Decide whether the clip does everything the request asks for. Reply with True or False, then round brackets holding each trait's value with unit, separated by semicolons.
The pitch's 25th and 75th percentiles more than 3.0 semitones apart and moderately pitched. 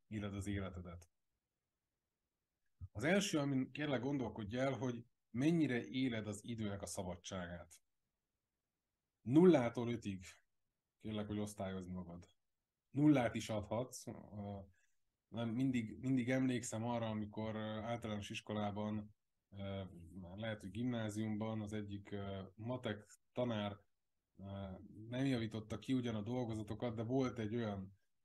False (3.5 semitones; 110 Hz)